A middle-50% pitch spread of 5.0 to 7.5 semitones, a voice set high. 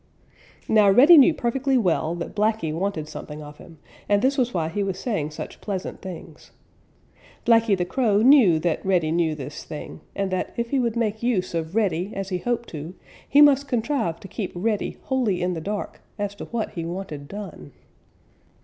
Yes: wide, 5.6 semitones; high, 200 Hz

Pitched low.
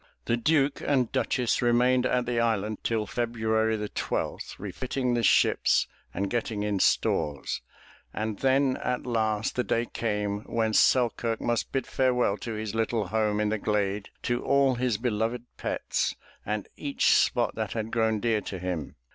Yes: low, 115 Hz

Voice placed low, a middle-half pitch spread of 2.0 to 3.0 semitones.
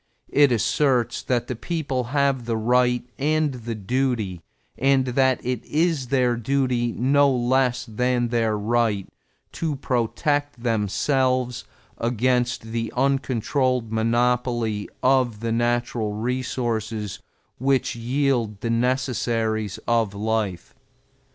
Yes: low, 120 Hz; narrow, 2.5 semitones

